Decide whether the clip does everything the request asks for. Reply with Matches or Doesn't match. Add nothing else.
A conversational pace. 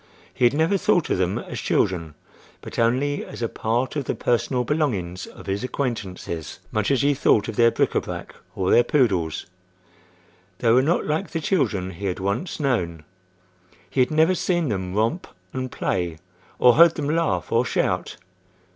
Matches